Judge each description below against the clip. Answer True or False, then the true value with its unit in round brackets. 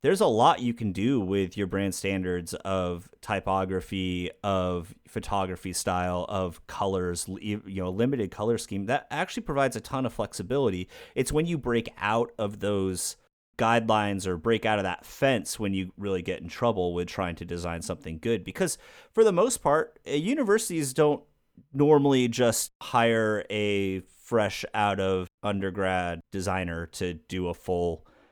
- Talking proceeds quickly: False (160 wpm)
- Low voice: True (95 Hz)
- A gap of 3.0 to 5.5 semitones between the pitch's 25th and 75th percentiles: True (4.2 semitones)